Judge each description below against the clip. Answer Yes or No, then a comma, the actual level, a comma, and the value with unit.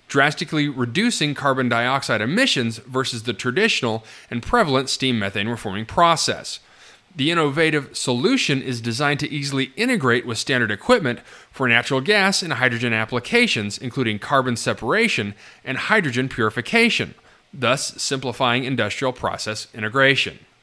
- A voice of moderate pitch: No, low, 130 Hz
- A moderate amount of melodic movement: Yes, average, 3.6 semitones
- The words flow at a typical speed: No, slow, 120 wpm